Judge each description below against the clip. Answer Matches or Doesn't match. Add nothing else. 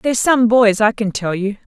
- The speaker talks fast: Matches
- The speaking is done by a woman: Matches